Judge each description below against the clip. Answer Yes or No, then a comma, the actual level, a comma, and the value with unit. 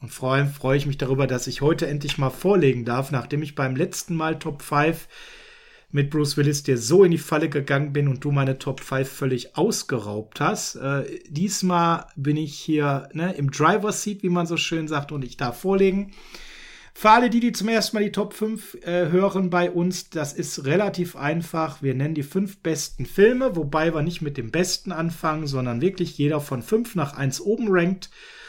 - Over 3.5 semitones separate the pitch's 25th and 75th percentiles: Yes, average, 4.9 semitones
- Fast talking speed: Yes, fast, 205 wpm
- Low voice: No, medium, 160 Hz